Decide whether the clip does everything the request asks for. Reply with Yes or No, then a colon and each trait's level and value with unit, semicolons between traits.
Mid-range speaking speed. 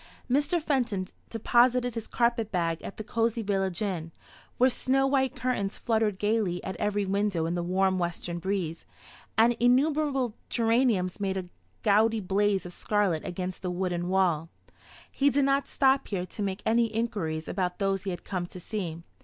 Yes: average, 170 wpm